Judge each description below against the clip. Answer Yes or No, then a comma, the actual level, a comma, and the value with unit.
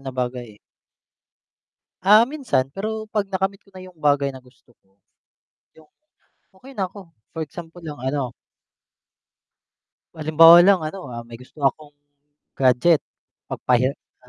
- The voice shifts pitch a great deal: Yes, wide, 6.7 semitones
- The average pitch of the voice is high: No, medium, 155 Hz